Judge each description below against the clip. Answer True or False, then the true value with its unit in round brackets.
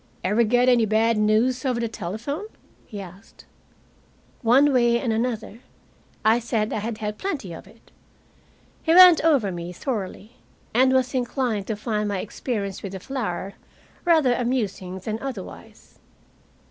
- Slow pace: False (145 wpm)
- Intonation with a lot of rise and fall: False (3.6 semitones)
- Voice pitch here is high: True (230 Hz)